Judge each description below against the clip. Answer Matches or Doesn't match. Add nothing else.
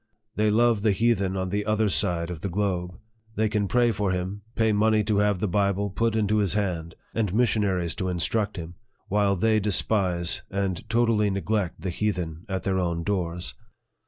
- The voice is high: Doesn't match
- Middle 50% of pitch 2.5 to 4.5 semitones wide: Matches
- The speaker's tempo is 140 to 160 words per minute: Doesn't match